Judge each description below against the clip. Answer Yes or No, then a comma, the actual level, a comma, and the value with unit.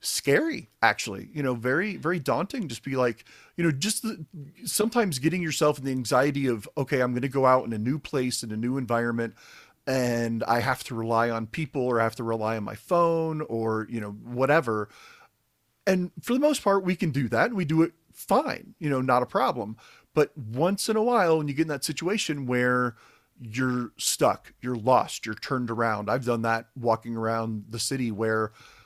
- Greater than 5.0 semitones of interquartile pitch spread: Yes, wide, 5.6 semitones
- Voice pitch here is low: Yes, low, 130 Hz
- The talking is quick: Yes, fast, 210 wpm